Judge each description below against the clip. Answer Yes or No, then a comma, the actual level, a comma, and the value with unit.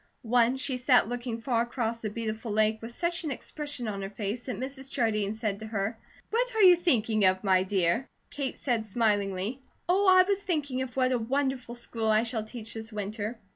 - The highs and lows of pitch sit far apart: No, average, 3.6 semitones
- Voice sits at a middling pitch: No, high, 235 Hz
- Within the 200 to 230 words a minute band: Yes, fast, 205 wpm